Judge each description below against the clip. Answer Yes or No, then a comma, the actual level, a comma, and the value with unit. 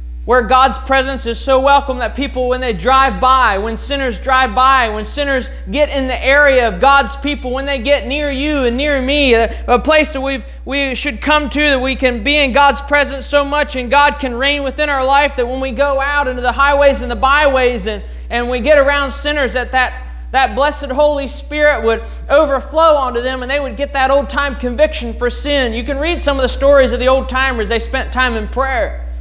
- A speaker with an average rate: No, fast, 230 wpm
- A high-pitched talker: Yes, very high, 270 Hz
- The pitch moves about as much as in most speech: No, narrow, 2.0 semitones